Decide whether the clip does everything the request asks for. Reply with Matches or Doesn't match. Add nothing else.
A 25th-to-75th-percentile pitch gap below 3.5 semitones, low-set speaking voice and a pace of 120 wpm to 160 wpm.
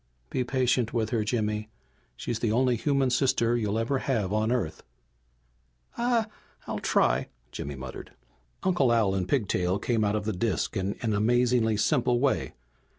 Matches